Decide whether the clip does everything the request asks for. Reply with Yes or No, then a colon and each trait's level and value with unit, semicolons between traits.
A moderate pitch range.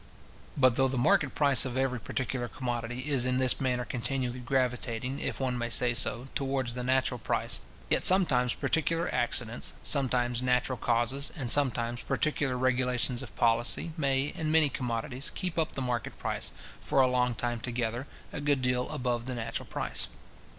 No: narrow, 2.0 semitones